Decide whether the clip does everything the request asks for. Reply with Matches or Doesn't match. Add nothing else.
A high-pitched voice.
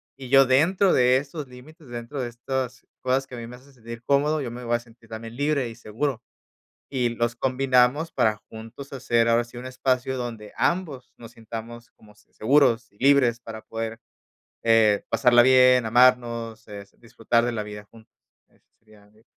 Doesn't match